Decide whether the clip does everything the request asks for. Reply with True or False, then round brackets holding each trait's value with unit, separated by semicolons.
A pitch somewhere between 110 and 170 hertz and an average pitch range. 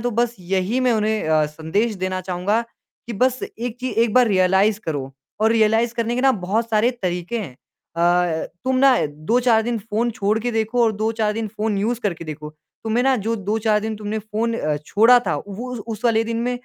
False (220 Hz; 3.2 semitones)